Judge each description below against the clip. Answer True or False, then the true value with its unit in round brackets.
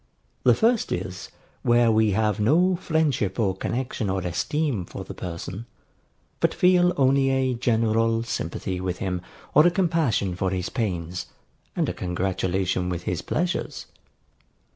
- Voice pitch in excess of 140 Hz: False (110 Hz)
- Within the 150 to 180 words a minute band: False (140 wpm)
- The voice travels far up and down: True (6.8 semitones)